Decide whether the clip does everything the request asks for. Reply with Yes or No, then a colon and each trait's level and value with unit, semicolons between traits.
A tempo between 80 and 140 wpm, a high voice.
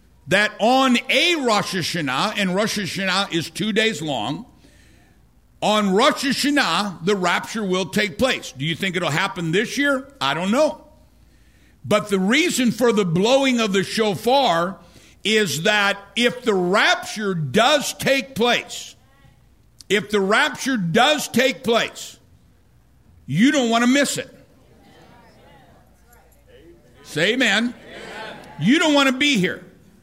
Yes: slow, 135 wpm; high, 215 Hz